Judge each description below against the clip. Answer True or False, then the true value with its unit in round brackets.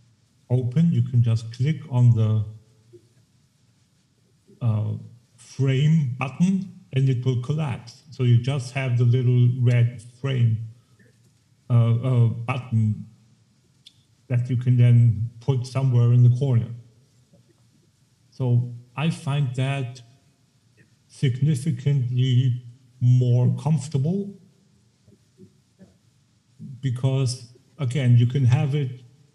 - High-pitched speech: False (125 Hz)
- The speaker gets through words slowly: True (95 wpm)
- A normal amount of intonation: False (2.2 semitones)